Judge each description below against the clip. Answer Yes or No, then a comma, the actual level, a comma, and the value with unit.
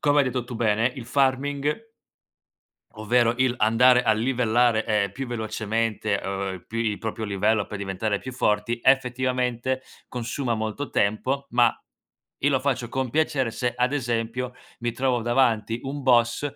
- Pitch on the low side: Yes, low, 120 Hz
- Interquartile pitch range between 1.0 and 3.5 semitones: Yes, average, 2.9 semitones